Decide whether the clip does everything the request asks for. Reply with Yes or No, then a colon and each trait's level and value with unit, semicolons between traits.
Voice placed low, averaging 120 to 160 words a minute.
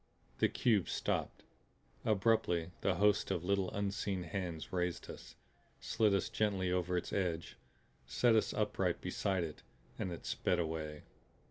Yes: very low, 90 Hz; average, 140 wpm